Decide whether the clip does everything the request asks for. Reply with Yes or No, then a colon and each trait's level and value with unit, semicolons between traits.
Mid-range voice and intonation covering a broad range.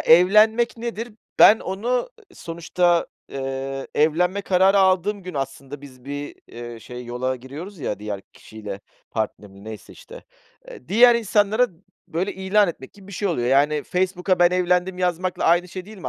Yes: medium, 175 Hz; wide, 6.3 semitones